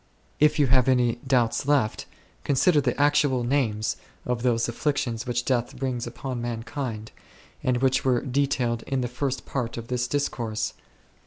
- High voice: No, low, 125 Hz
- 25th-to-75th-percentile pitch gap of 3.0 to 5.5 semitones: No, narrow, 2.4 semitones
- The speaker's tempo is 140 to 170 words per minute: Yes, average, 160 wpm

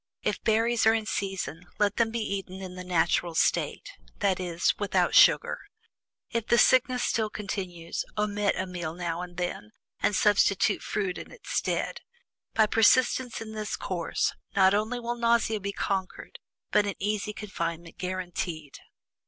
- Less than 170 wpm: Yes, average, 155 wpm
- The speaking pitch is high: Yes, high, 200 Hz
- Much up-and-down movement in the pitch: No, average, 3.4 semitones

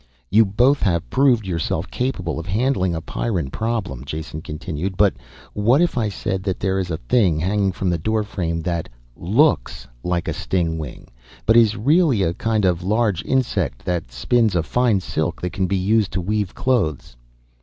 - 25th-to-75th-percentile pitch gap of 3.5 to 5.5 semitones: Yes, average, 4.8 semitones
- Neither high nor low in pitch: No, very low, 95 Hz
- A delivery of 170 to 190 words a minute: Yes, average, 175 wpm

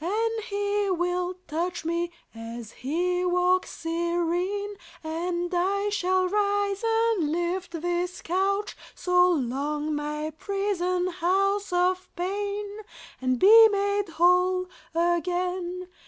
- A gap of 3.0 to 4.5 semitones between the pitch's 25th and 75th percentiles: No, narrow, 2.6 semitones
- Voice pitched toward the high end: Yes, very high, 360 Hz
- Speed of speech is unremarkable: No, slow, 110 wpm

